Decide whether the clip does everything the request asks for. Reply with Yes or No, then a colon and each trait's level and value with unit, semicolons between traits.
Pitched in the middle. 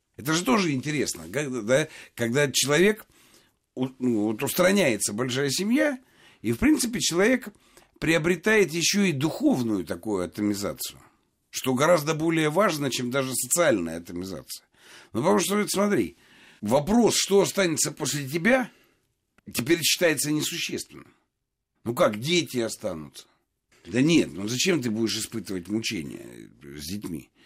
Yes: medium, 150 Hz